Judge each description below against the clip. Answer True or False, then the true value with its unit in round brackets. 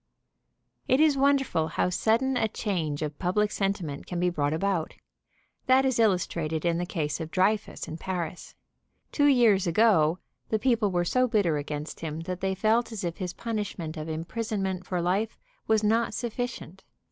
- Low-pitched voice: False (190 Hz)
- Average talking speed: True (180 wpm)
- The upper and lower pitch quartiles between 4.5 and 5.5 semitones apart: True (5.2 semitones)